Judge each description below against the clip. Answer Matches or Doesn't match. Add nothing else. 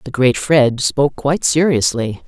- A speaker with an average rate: Matches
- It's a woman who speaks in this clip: Matches